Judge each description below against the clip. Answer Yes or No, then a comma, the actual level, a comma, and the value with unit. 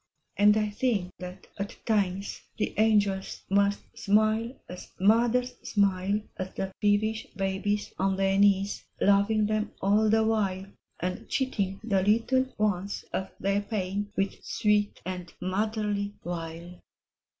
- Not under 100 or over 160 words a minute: Yes, slow, 135 wpm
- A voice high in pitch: Yes, high, 205 Hz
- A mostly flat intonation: Yes, narrow, 2.0 semitones